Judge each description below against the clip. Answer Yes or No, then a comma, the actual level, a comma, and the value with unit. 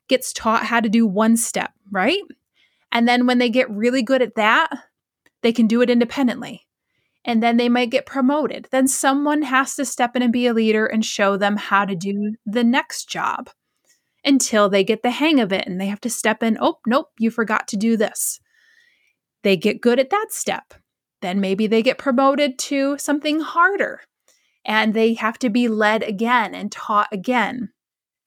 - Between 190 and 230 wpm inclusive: Yes, average, 195 wpm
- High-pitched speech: Yes, high, 240 Hz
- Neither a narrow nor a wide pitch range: Yes, average, 3.7 semitones